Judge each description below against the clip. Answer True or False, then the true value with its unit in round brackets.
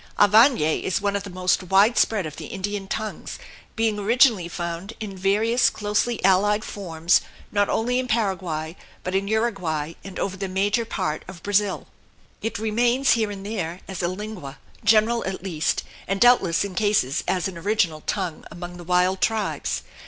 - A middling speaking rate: True (170 wpm)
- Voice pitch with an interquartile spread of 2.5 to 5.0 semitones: True (3.2 semitones)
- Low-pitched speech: False (195 Hz)